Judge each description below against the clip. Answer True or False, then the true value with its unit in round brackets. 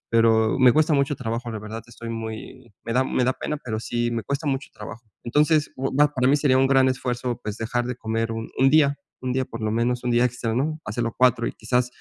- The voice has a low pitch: True (125 Hz)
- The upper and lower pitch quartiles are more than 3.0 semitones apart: False (2.6 semitones)